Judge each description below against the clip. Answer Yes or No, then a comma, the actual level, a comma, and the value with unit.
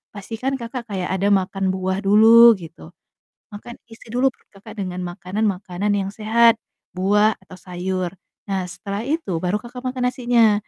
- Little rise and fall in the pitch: No, average, 3.6 semitones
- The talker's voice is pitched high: Yes, high, 205 Hz